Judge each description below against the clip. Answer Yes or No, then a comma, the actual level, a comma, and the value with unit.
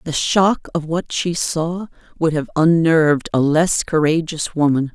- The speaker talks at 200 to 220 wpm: No, average, 160 wpm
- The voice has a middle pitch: Yes, medium, 160 Hz